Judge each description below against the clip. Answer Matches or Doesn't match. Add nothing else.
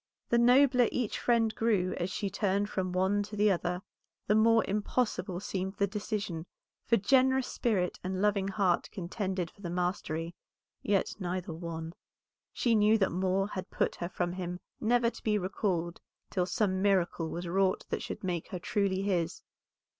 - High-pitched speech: Matches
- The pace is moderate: Matches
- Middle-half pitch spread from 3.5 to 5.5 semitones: Doesn't match